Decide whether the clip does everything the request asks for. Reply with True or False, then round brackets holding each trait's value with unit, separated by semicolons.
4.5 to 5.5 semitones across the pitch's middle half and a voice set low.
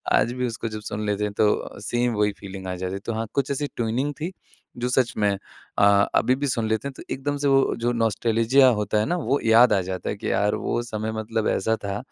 False (3.3 semitones; 115 Hz)